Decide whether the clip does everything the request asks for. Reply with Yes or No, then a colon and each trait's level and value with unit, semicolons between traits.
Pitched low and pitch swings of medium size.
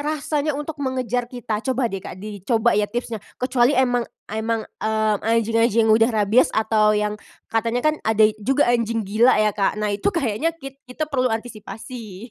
No: high, 230 Hz; average, 3.0 semitones